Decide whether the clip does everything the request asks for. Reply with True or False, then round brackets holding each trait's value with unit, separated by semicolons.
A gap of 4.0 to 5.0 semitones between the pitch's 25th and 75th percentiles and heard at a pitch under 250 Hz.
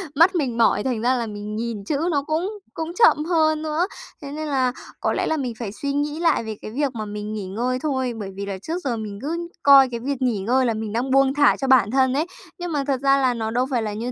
False (4.7 semitones; 260 Hz)